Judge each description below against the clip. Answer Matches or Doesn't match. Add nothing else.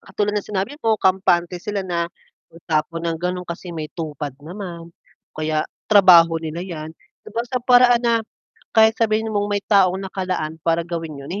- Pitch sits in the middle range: Matches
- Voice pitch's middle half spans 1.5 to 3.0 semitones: Doesn't match